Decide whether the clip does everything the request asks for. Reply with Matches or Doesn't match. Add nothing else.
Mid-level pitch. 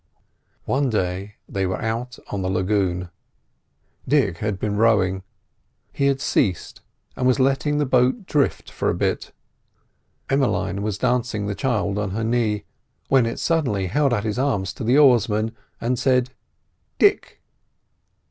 Doesn't match